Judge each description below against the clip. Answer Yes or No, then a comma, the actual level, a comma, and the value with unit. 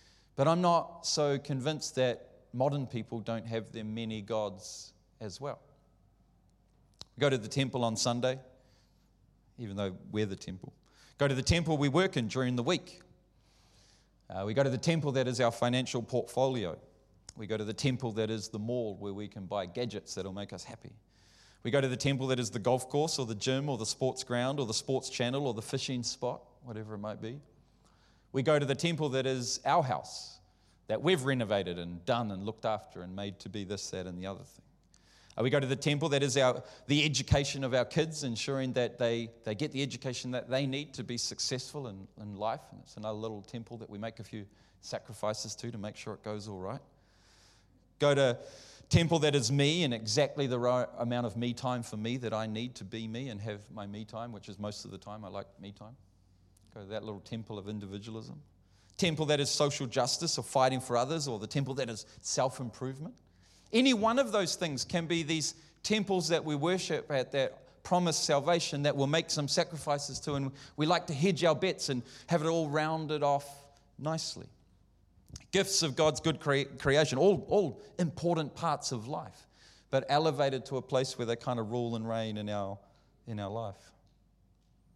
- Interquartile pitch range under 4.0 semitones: No, average, 4.8 semitones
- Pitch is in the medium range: No, low, 125 Hz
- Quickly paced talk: Yes, fast, 210 wpm